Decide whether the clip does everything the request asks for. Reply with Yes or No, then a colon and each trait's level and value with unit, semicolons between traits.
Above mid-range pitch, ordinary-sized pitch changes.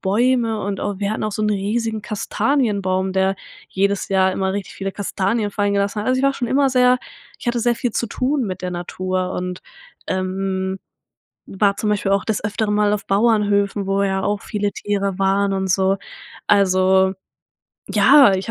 No: high, 200 Hz; narrow, 2.1 semitones